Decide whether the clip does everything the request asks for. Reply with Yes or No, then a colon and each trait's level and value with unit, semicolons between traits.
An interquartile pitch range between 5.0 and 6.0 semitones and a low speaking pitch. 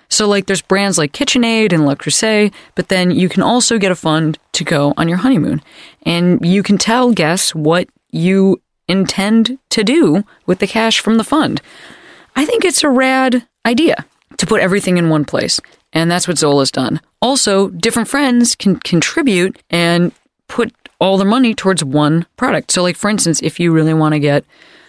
No: wide, 5.5 semitones; high, 195 Hz